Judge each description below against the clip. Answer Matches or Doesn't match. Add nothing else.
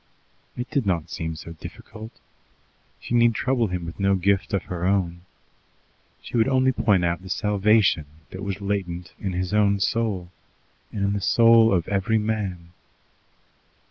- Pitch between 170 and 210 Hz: Doesn't match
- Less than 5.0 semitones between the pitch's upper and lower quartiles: Matches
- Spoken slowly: Doesn't match